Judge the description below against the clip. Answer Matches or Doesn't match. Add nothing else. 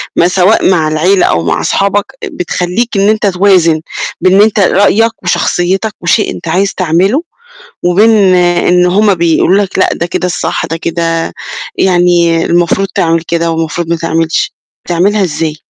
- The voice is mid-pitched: Matches